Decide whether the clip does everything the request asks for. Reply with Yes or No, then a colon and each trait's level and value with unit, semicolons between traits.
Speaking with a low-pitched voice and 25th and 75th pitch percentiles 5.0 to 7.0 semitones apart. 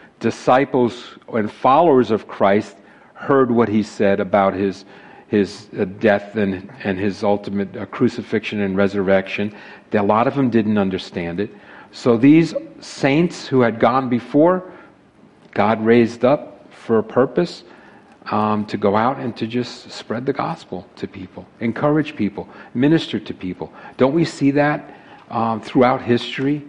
Yes: low, 115 Hz; wide, 5.4 semitones